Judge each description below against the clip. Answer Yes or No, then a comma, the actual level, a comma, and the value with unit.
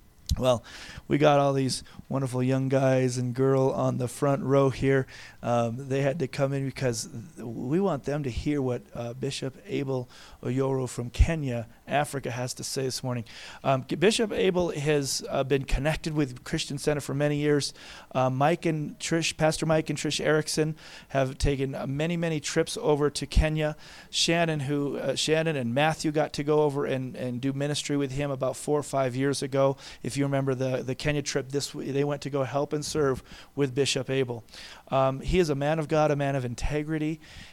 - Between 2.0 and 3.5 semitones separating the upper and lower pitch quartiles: Yes, narrow, 2.4 semitones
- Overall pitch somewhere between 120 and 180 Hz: Yes, medium, 140 Hz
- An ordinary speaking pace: Yes, average, 195 wpm